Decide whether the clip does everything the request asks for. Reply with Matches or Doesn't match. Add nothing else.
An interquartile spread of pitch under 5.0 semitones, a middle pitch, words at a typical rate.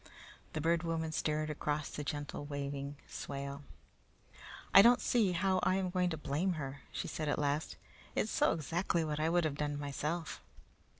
Matches